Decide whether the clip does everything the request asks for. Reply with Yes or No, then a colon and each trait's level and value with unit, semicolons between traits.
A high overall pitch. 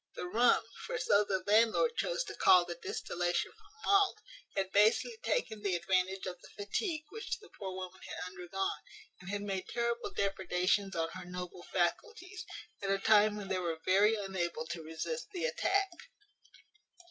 Yes: high, 195 Hz